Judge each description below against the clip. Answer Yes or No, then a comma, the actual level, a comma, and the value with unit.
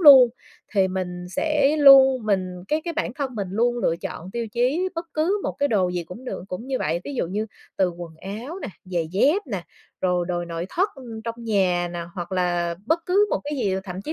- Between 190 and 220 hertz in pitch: Yes, high, 210 Hz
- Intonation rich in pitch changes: Yes, wide, 7.5 semitones